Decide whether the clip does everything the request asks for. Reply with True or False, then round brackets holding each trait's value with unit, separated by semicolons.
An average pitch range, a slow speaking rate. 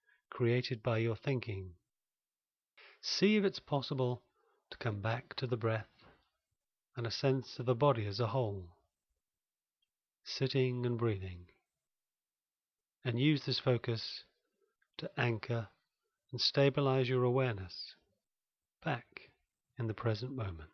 True (3.1 semitones; 120 wpm)